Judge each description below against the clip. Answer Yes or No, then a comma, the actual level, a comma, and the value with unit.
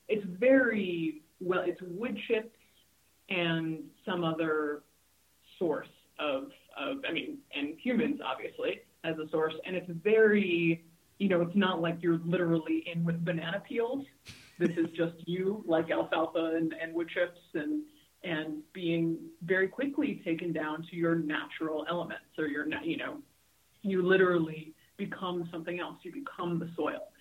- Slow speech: No, average, 150 wpm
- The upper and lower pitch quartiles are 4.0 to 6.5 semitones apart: Yes, average, 5.0 semitones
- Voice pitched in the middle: Yes, medium, 175 Hz